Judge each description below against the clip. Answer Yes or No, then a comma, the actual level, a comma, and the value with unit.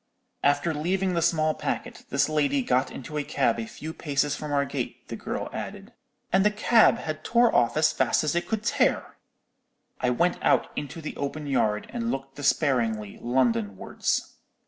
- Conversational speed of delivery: Yes, average, 180 wpm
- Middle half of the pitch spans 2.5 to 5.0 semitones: Yes, average, 4.4 semitones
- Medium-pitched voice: Yes, medium, 145 Hz